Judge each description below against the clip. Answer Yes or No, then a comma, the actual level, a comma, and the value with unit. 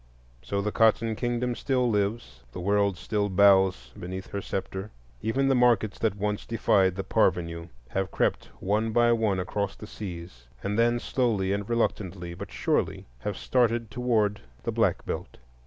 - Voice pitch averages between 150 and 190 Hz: No, low, 105 Hz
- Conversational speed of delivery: Yes, average, 160 wpm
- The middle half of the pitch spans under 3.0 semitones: No, average, 3.4 semitones